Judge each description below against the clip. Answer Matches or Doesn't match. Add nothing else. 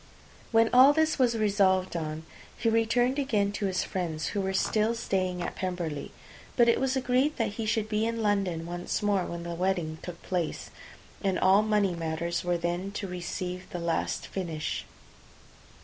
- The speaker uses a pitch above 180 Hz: Matches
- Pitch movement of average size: Matches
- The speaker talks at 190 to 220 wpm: Doesn't match